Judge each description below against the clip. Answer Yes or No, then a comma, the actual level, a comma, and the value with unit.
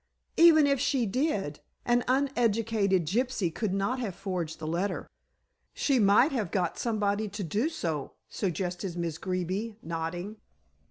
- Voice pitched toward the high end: Yes, high, 200 Hz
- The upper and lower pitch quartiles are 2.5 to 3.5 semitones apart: No, wide, 5.5 semitones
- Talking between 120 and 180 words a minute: Yes, average, 140 wpm